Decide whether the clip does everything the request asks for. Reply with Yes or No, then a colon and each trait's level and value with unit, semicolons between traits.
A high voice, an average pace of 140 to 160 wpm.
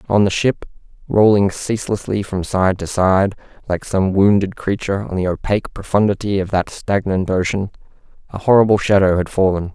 No: low, 100 Hz; average, 150 wpm